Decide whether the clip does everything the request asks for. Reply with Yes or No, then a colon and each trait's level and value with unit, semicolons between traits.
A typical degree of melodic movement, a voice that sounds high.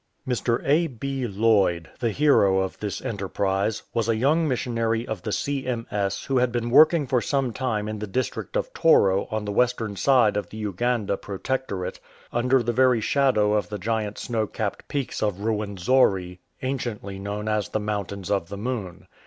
No: average, 3.9 semitones; low, 110 Hz